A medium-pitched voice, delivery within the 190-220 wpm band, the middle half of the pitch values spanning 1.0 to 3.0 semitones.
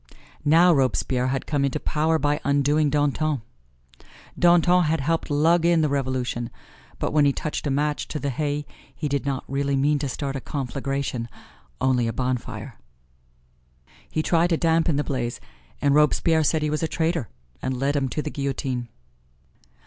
No: medium, 145 Hz; average, 170 wpm; narrow, 2.6 semitones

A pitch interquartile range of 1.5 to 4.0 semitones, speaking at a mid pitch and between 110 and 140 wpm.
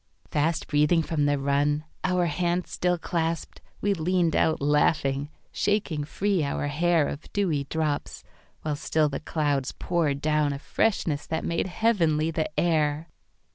Yes: average, 2.9 semitones; medium, 155 Hz; slow, 135 wpm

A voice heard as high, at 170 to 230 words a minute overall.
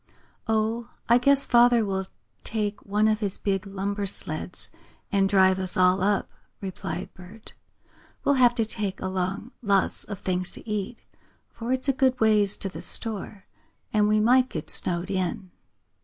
No: high, 205 Hz; average, 160 wpm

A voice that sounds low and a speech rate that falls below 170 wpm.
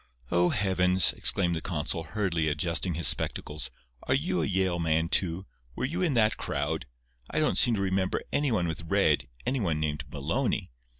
No: very low, 90 Hz; average, 175 wpm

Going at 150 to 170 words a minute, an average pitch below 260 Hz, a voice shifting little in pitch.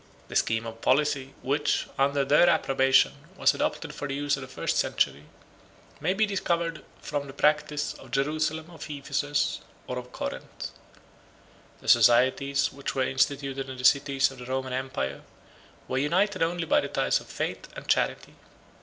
Yes: average, 165 wpm; medium, 140 Hz; narrow, 2.2 semitones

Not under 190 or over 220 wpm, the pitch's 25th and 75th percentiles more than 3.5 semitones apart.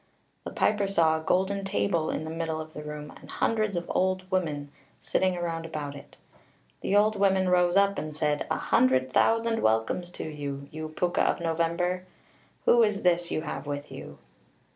Yes: average, 195 wpm; average, 3.9 semitones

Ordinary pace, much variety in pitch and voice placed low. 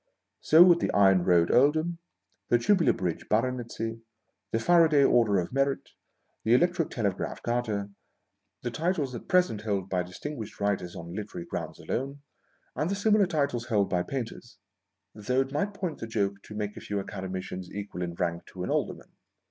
Yes: average, 170 wpm; wide, 6.5 semitones; low, 115 Hz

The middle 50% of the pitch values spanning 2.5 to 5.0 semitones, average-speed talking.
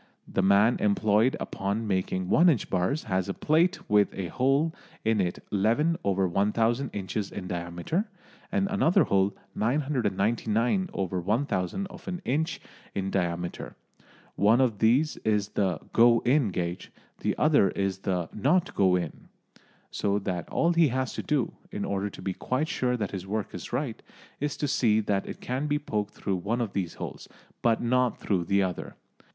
No: wide, 5.5 semitones; average, 165 wpm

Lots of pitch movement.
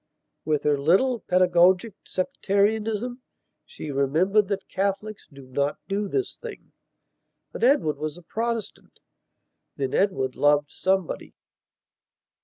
Yes: wide, 6.2 semitones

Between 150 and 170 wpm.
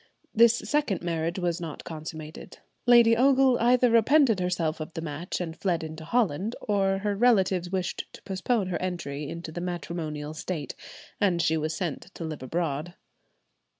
Yes: average, 160 wpm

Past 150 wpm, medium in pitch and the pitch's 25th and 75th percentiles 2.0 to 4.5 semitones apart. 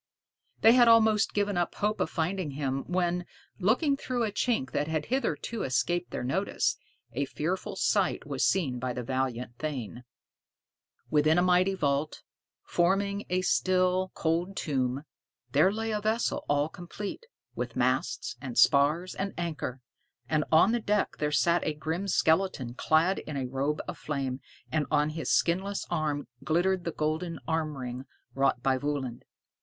No: average, 160 wpm; medium, 165 Hz; average, 5.1 semitones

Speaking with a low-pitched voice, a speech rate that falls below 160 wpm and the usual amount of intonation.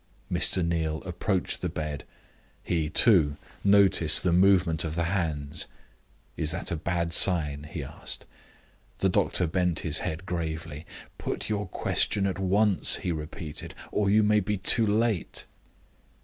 Yes: very low, 85 Hz; average, 145 wpm; average, 3.7 semitones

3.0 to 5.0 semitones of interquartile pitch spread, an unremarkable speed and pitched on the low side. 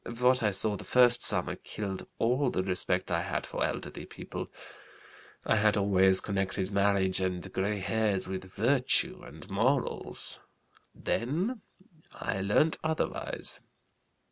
No: average, 4.7 semitones; slow, 130 wpm; low, 105 Hz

